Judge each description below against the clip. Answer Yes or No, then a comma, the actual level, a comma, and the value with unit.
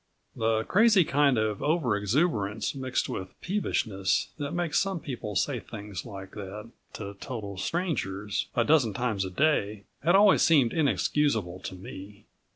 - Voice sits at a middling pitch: No, low, 115 Hz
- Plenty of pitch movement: Yes, wide, 6.8 semitones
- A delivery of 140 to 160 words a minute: Yes, average, 150 wpm